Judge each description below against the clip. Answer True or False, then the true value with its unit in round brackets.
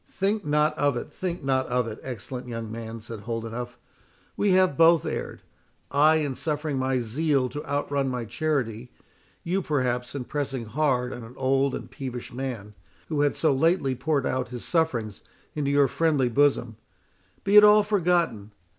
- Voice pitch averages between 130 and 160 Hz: True (135 Hz)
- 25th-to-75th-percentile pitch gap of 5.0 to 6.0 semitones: False (4.0 semitones)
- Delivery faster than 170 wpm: False (165 wpm)